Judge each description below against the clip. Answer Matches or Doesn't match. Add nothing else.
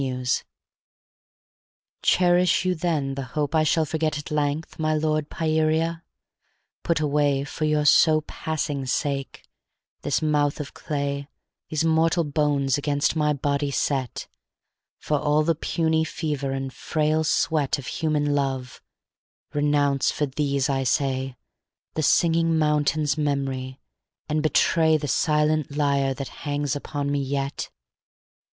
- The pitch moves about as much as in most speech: Doesn't match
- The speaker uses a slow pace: Matches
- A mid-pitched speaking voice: Matches